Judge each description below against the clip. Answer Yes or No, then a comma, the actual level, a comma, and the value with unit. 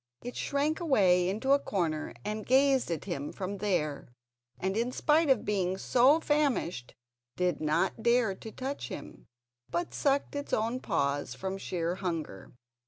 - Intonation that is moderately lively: No, wide, 7.1 semitones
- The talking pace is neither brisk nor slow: Yes, average, 155 wpm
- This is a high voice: Yes, high, 210 Hz